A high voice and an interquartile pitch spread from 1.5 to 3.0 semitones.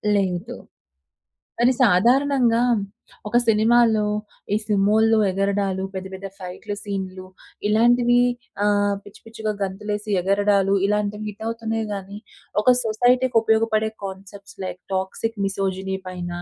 Yes: high, 205 Hz; narrow, 2.6 semitones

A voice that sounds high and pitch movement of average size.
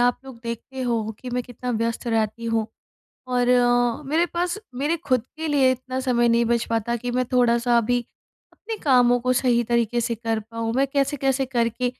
No: high, 245 Hz; narrow, 1.8 semitones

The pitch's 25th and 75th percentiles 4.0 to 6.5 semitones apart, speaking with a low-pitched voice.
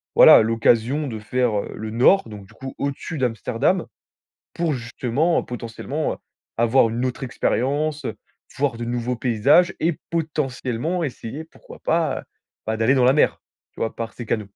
Yes: average, 4.5 semitones; low, 125 Hz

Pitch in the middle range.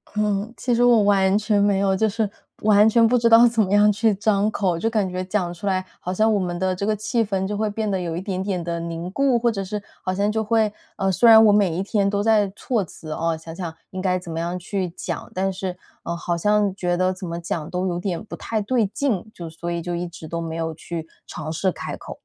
No: high, 195 Hz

